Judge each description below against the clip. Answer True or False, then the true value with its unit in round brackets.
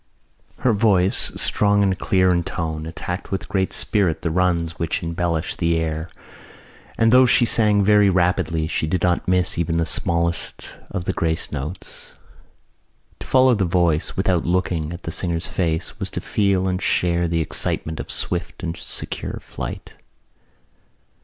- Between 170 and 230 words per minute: False (160 wpm)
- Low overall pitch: True (90 Hz)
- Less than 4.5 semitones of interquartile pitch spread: True (2.5 semitones)